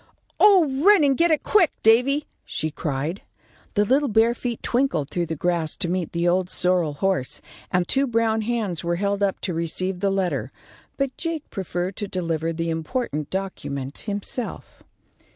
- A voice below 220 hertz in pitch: Yes, high, 190 Hz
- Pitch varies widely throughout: Yes, wide, 6.0 semitones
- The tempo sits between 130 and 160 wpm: No, average, 170 wpm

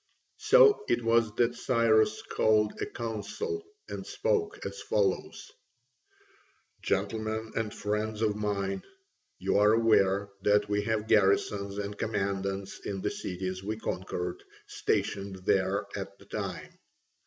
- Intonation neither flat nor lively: No, narrow, 2.1 semitones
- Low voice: Yes, low, 105 Hz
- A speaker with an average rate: No, slow, 125 wpm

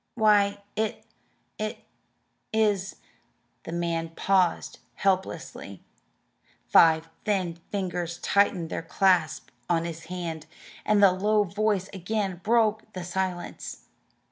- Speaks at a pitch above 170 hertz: Yes, high, 190 Hz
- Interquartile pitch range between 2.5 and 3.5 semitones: Yes, average, 3.2 semitones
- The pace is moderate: No, slow, 110 wpm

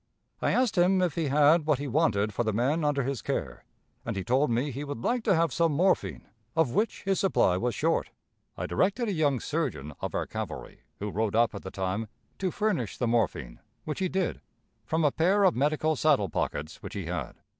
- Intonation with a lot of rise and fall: Yes, wide, 7.0 semitones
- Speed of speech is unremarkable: No, fast, 215 wpm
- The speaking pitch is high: No, medium, 145 Hz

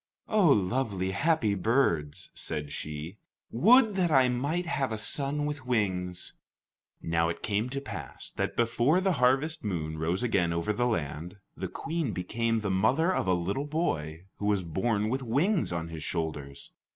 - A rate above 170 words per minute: No, average, 165 wpm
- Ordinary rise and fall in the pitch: No, wide, 8.2 semitones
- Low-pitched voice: Yes, low, 110 Hz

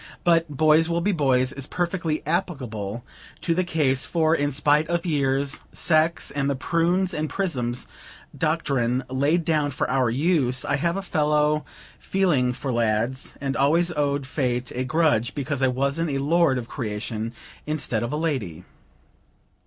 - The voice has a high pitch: No, medium, 145 Hz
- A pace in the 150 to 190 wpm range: Yes, average, 160 wpm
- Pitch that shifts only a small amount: No, average, 4.2 semitones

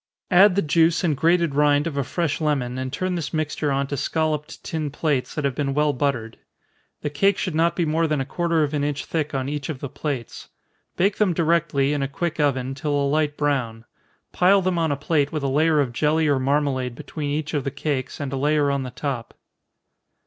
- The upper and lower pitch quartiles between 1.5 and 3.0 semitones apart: Yes, narrow, 2.6 semitones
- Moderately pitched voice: Yes, medium, 145 Hz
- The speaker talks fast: Yes, fast, 225 wpm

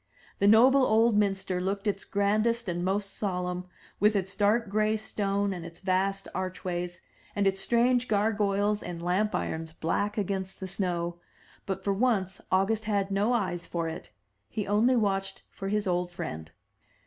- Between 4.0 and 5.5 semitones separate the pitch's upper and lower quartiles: No, narrow, 2.4 semitones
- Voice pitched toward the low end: No, high, 195 Hz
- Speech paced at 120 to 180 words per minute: Yes, average, 165 wpm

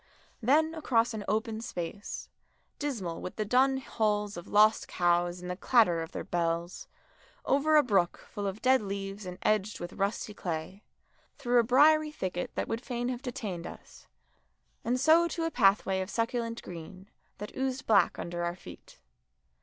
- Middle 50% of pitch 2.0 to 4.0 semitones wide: No, wide, 5.5 semitones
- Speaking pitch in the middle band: No, high, 215 Hz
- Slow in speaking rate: No, average, 170 wpm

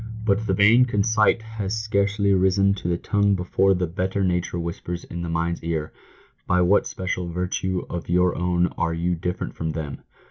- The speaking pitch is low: Yes, very low, 90 Hz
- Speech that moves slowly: No, average, 185 wpm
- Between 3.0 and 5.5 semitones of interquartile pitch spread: No, narrow, 2.6 semitones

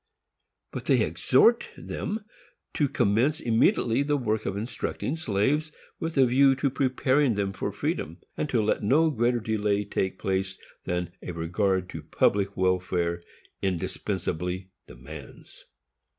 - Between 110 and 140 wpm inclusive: Yes, slow, 135 wpm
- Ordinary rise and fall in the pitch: No, wide, 6.3 semitones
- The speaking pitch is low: Yes, low, 105 Hz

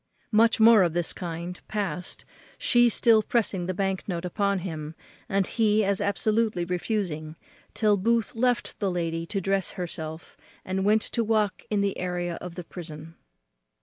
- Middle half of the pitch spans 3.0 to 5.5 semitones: Yes, average, 3.6 semitones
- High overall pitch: Yes, high, 195 Hz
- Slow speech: No, average, 160 wpm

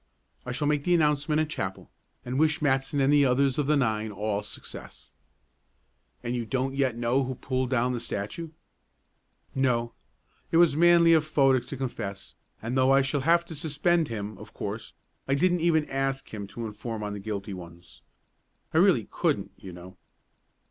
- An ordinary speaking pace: Yes, average, 180 wpm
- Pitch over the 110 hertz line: Yes, low, 135 Hz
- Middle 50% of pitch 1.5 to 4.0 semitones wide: No, average, 4.8 semitones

